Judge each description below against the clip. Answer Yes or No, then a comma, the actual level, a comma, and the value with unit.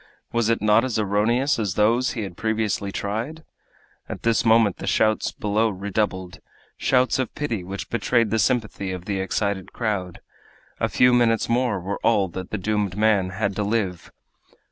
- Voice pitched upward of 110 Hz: No, low, 105 Hz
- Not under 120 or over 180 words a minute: Yes, average, 170 wpm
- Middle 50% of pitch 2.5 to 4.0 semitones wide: Yes, average, 2.8 semitones